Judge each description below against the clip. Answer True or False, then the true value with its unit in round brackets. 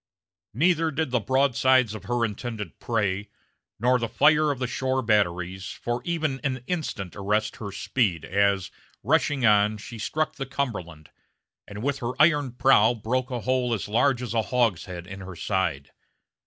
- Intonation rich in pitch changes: False (4.5 semitones)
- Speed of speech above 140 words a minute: True (165 wpm)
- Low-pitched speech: True (120 Hz)